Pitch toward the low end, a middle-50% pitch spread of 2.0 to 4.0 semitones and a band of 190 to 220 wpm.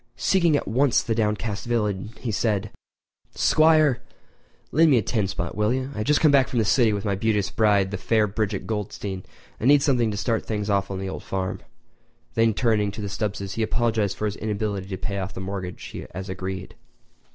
Yes: low, 105 Hz; average, 3.0 semitones; average, 200 wpm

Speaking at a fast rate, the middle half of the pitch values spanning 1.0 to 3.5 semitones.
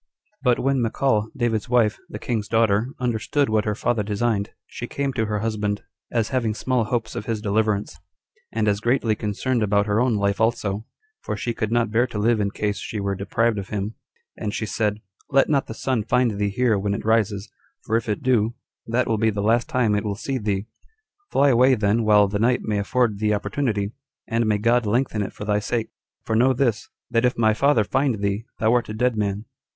Yes: fast, 215 wpm; narrow, 2.5 semitones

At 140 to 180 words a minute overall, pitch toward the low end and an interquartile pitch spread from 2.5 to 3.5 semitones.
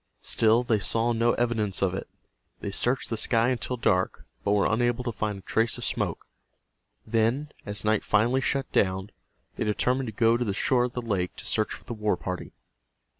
No: average, 200 wpm; low, 115 Hz; average, 2.8 semitones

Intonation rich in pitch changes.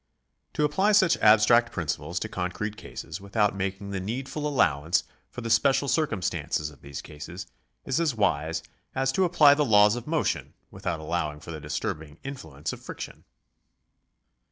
Yes: wide, 8.8 semitones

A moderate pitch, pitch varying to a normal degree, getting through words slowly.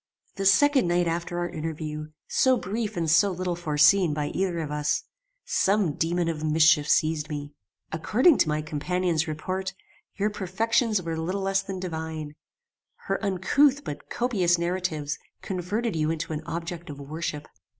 No: medium, 175 Hz; average, 3.8 semitones; average, 155 wpm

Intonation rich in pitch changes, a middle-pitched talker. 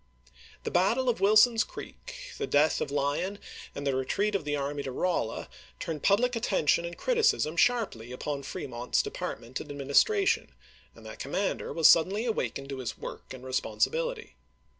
Yes: wide, 8.1 semitones; medium, 160 Hz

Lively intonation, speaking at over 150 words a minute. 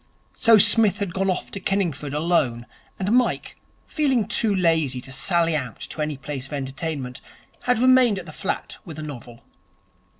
Yes: wide, 6.4 semitones; average, 170 wpm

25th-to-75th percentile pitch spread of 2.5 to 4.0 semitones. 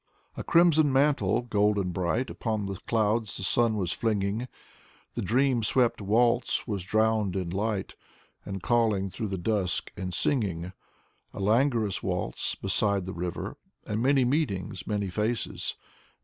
Yes: average, 3.6 semitones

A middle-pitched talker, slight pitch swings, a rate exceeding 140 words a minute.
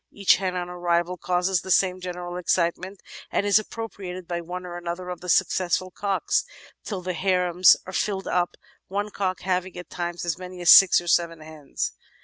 Yes: medium, 180 Hz; narrow, 1.2 semitones; average, 185 wpm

